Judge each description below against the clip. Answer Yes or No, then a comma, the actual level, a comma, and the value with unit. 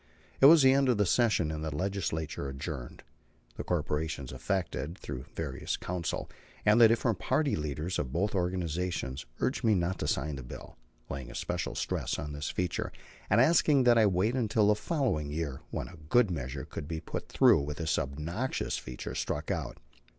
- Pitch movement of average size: No, wide, 6.7 semitones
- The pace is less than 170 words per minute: No, average, 180 wpm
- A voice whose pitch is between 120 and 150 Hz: No, very low, 85 Hz